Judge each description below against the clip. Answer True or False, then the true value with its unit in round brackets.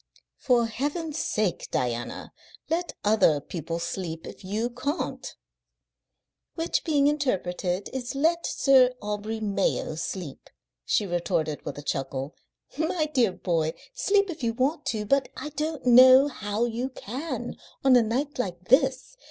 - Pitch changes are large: True (7.4 semitones)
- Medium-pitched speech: False (235 Hz)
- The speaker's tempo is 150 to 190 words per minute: False (140 wpm)